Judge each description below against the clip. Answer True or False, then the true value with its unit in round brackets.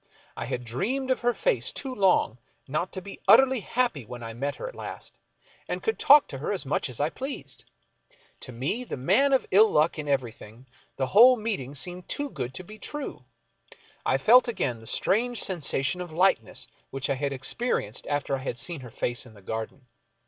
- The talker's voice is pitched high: False (155 Hz)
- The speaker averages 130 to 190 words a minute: False (200 wpm)